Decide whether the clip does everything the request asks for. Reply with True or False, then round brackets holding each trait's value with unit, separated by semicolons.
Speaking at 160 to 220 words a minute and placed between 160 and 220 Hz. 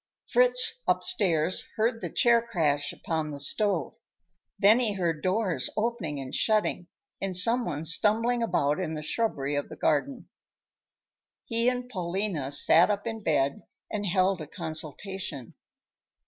False (140 wpm; 190 Hz)